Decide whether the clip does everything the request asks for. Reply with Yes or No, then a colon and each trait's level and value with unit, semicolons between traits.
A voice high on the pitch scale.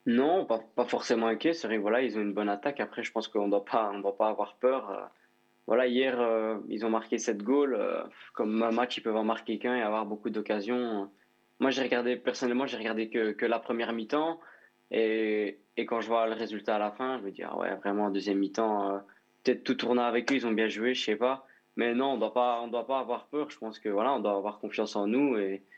No: low, 115 Hz